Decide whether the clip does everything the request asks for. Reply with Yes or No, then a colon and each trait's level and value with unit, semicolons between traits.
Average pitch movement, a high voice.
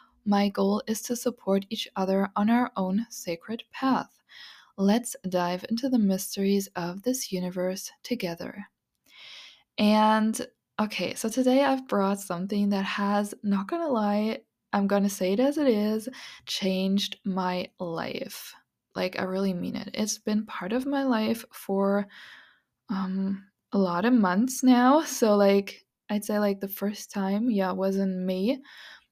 Yes: average, 3.1 semitones; high, 205 Hz